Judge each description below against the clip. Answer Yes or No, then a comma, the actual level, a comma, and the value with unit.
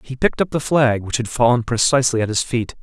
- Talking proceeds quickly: Yes, fast, 255 wpm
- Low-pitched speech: Yes, low, 120 Hz